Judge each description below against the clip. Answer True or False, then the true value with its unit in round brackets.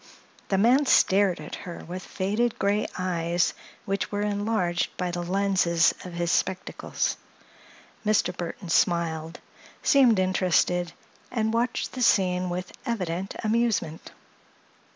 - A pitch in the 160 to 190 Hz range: True (185 Hz)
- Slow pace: True (120 wpm)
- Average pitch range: True (3.3 semitones)